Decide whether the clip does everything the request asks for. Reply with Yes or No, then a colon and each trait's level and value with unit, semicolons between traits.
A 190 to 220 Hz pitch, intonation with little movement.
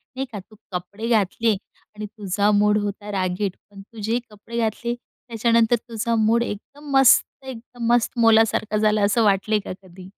Yes: high, 215 Hz; narrow, 2.3 semitones